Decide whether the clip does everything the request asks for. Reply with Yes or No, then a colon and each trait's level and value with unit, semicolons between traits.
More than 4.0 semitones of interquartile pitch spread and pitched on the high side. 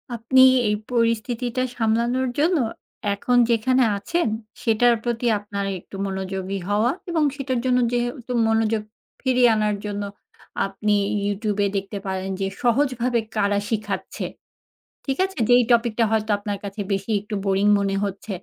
No: average, 3.3 semitones; high, 225 Hz